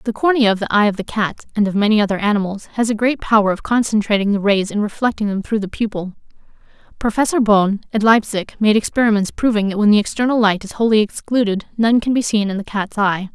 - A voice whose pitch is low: No, high, 210 Hz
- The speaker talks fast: Yes, fast, 225 wpm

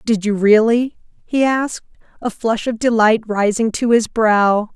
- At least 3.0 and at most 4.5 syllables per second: Yes, 4.2 syllables/s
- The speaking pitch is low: No, high, 225 Hz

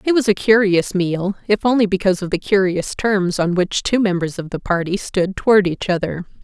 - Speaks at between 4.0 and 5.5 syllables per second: Yes, 5.3 syllables/s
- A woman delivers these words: Yes, female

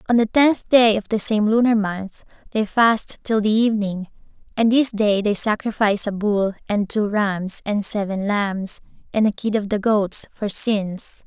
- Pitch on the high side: Yes, high, 210 Hz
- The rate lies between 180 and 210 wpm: Yes, average, 185 wpm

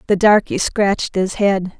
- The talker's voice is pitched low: No, high, 200 Hz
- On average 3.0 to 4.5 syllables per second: Yes, 4.4 syllables/s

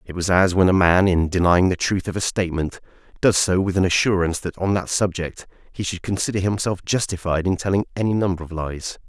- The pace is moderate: No, fast, 220 wpm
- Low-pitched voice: Yes, very low, 90 Hz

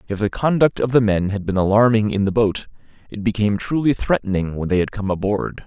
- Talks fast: Yes, fast, 220 wpm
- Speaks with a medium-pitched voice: No, low, 105 Hz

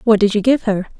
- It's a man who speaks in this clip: No, female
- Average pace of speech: No, fast, 300 wpm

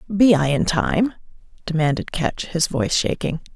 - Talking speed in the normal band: Yes, average, 150 wpm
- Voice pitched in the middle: Yes, medium, 170 Hz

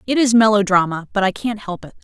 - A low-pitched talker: No, high, 205 Hz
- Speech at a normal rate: No, fast, 235 wpm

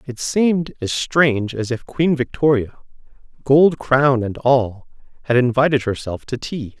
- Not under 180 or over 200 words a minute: No, average, 150 wpm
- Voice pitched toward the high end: No, low, 130 Hz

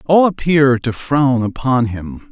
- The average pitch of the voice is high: No, low, 130 Hz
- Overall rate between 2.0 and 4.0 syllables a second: Yes, 3.7 syllables/s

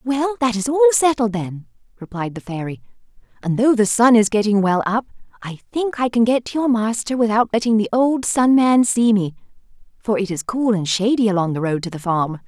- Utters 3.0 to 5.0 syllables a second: No, 5.4 syllables/s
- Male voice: No, female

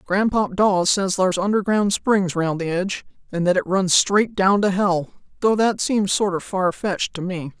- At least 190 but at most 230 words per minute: Yes, average, 195 wpm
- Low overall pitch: No, high, 190 Hz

